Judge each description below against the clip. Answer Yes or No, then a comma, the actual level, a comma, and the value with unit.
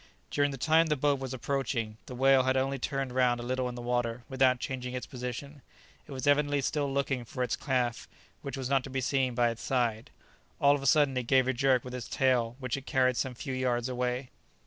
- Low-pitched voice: Yes, low, 130 Hz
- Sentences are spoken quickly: Yes, fast, 235 wpm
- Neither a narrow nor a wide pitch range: No, narrow, 1.7 semitones